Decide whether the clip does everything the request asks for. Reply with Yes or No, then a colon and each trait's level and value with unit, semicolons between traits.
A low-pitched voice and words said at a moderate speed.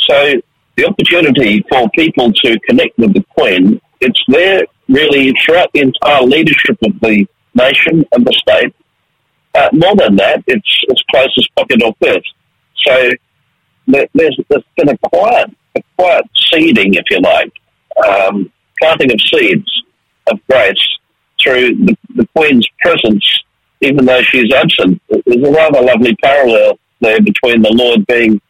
No: medium, 170 Hz; average, 150 wpm